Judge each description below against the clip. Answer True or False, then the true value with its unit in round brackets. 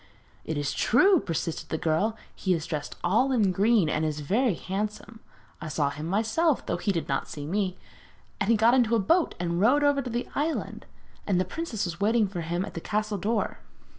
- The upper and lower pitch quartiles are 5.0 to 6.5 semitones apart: True (5.6 semitones)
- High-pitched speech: True (200 Hz)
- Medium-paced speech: False (210 wpm)